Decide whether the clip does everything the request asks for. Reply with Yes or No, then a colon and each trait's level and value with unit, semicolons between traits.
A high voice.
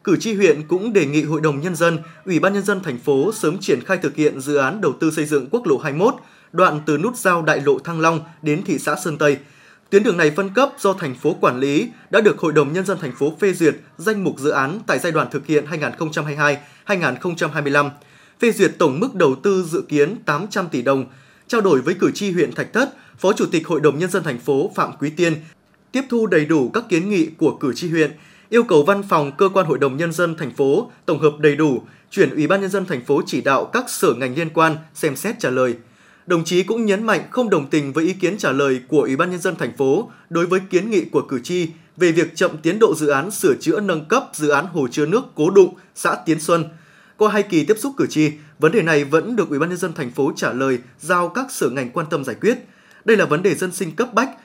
No: medium, 165 Hz